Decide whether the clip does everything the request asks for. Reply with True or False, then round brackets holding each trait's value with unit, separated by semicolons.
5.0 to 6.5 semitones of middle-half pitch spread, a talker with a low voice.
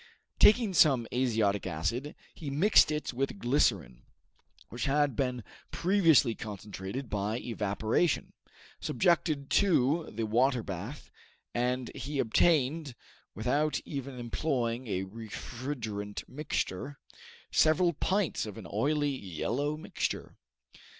True (5.3 semitones; 125 Hz)